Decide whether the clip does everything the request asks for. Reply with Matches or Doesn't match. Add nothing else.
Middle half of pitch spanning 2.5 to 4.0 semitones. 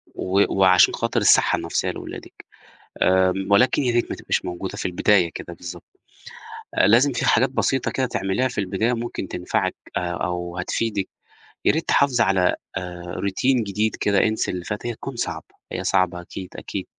Doesn't match